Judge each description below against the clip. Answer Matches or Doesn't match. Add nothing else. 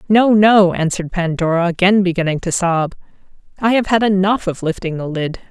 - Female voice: Matches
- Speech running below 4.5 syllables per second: Doesn't match